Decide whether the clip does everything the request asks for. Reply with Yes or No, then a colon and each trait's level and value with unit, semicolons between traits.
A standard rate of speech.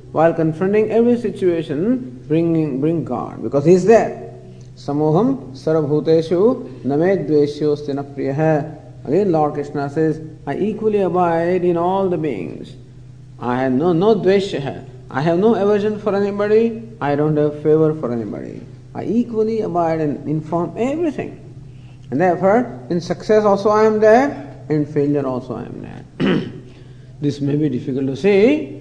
Yes: average, 145 wpm